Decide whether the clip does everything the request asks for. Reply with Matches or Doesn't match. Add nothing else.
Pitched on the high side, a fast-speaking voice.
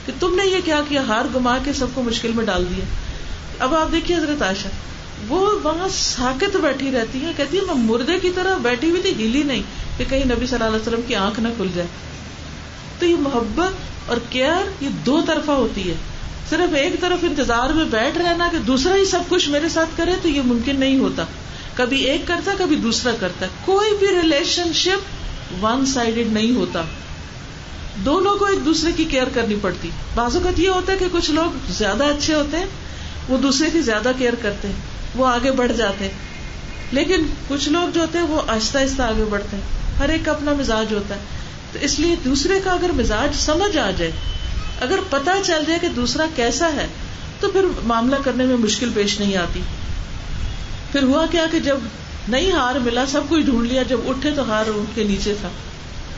Matches